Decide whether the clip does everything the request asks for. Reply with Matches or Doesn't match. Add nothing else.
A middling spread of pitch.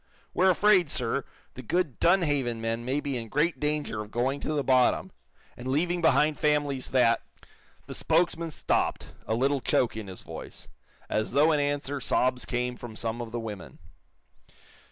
Matches